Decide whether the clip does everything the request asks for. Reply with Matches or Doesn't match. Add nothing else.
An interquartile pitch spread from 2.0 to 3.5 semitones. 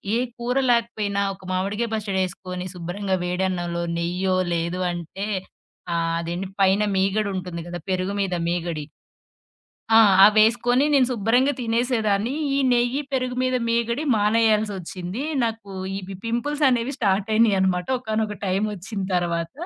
Doesn't match